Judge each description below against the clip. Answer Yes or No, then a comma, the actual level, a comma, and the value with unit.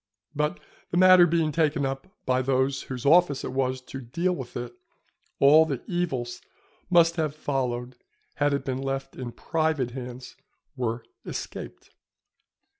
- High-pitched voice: No, low, 135 Hz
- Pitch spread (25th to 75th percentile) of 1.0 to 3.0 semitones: No, average, 3.7 semitones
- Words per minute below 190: Yes, average, 150 wpm